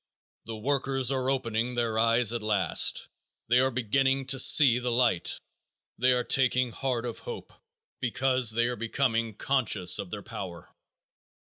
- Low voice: Yes, low, 120 Hz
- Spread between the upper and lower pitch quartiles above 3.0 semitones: No, narrow, 2.6 semitones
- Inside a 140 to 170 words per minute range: Yes, average, 150 wpm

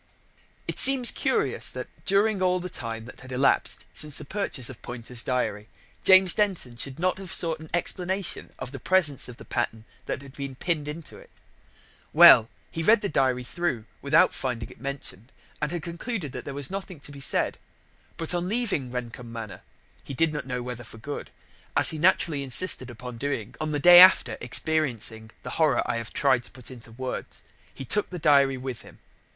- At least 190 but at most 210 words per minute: Yes, average, 195 wpm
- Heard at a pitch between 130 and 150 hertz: Yes, medium, 140 Hz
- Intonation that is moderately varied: No, wide, 5.9 semitones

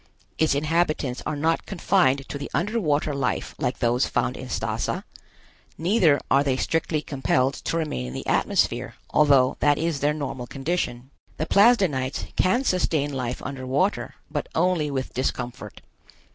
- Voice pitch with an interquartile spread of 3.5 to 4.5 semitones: Yes, average, 3.9 semitones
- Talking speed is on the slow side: No, average, 155 wpm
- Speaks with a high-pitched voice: No, medium, 145 Hz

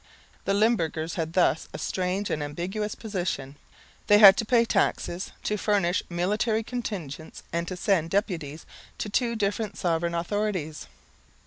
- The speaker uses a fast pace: No, average, 140 wpm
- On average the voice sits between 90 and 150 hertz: No, high, 190 Hz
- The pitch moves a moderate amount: Yes, average, 3.9 semitones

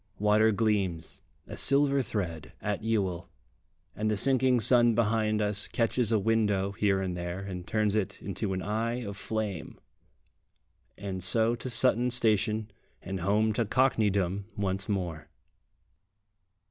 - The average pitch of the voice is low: Yes, low, 105 Hz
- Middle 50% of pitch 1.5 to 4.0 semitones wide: Yes, average, 2.8 semitones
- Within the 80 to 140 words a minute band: Yes, slow, 135 wpm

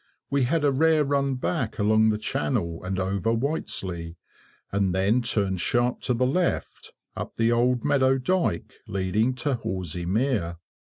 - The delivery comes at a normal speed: Yes, average, 155 wpm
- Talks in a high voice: No, low, 115 Hz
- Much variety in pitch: Yes, wide, 5.9 semitones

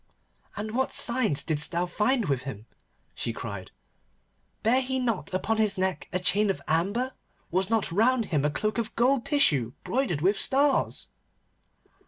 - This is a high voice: Yes, high, 205 Hz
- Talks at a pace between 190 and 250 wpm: No, average, 160 wpm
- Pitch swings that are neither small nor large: No, wide, 7.1 semitones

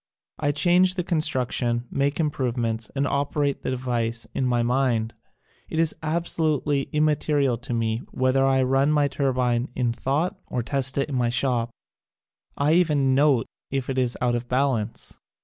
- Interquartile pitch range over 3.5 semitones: No, average, 3.2 semitones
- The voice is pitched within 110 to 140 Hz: Yes, low, 135 Hz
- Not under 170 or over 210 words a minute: No, average, 160 wpm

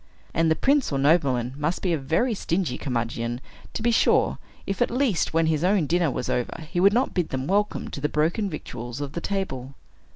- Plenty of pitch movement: Yes, wide, 6.3 semitones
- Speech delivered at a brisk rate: Yes, fast, 215 wpm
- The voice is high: No, medium, 160 Hz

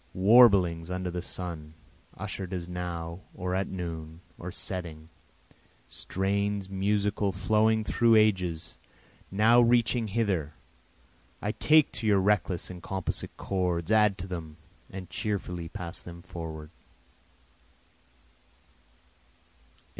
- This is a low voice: Yes, very low, 95 Hz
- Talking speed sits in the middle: No, slow, 110 wpm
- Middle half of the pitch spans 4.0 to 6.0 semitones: No, average, 3.2 semitones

